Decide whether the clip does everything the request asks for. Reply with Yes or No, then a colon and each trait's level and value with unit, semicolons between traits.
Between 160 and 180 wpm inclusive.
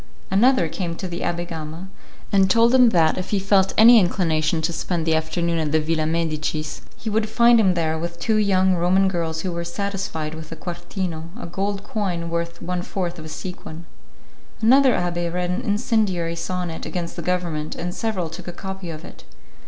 No: average, 195 wpm